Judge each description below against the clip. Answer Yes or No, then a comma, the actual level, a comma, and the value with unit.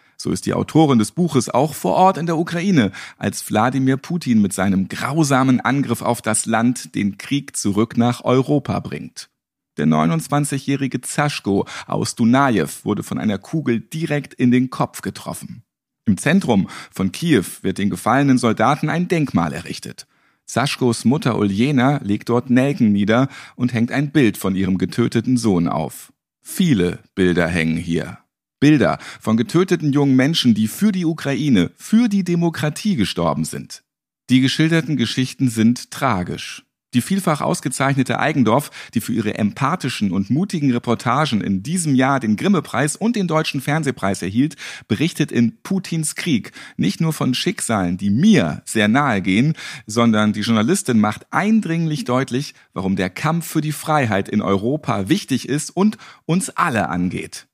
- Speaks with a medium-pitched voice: No, low, 130 Hz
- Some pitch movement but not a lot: No, wide, 5.9 semitones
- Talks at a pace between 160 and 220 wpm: No, average, 150 wpm